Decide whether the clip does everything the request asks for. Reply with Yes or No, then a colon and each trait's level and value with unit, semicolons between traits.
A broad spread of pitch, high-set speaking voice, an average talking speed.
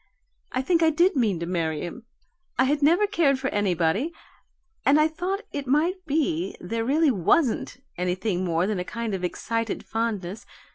Yes: wide, 8.7 semitones; high, 235 Hz; average, 175 wpm